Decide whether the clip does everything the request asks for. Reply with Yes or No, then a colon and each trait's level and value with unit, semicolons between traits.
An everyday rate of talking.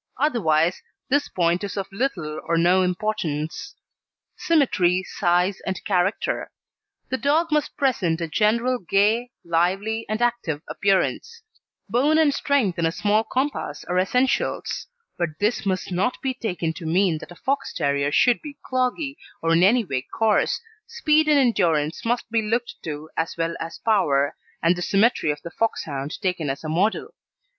Yes: average, 160 wpm